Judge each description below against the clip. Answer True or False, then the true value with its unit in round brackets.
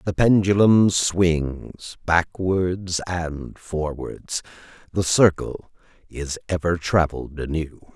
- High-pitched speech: False (85 Hz)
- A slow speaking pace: True (90 wpm)